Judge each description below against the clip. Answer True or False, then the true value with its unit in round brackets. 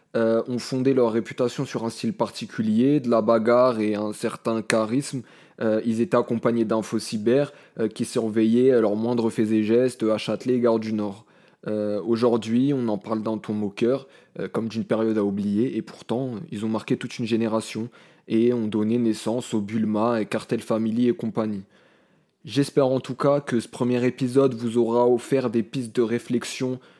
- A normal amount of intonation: False (2.1 semitones)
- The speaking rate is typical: True (190 wpm)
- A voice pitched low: True (115 Hz)